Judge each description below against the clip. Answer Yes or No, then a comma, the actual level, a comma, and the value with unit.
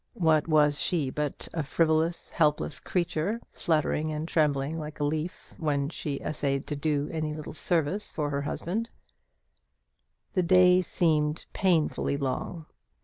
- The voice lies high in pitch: No, medium, 155 Hz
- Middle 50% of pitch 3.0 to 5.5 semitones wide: No, narrow, 2.4 semitones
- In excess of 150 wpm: No, average, 140 wpm